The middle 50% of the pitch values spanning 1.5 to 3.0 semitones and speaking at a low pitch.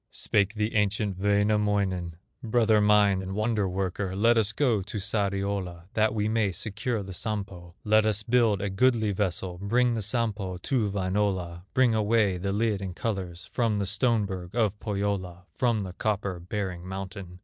Yes: narrow, 2.4 semitones; low, 100 Hz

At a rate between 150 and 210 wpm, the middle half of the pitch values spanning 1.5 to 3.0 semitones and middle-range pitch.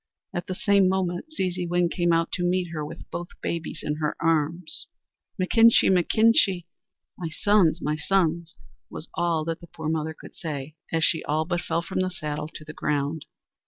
Yes: average, 180 wpm; narrow, 2.6 semitones; medium, 170 Hz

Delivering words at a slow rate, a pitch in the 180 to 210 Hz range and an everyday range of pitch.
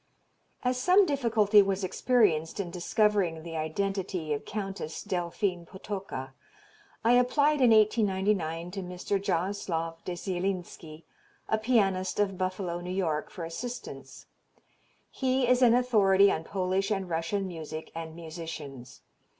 Yes: slow, 125 wpm; high, 190 Hz; average, 4.0 semitones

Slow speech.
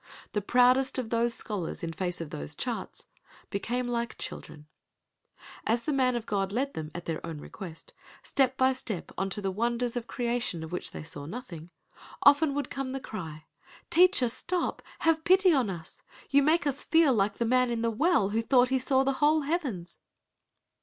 No: average, 185 wpm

